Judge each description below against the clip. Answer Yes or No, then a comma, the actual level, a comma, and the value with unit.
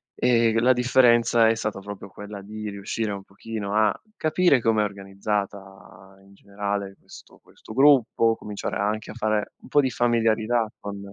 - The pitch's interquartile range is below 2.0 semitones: No, average, 2.7 semitones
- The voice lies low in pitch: Yes, low, 110 Hz